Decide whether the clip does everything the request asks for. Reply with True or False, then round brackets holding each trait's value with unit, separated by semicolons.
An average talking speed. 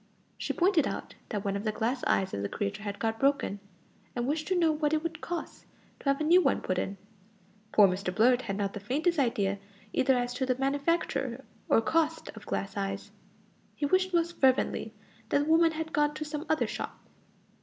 False (210 wpm)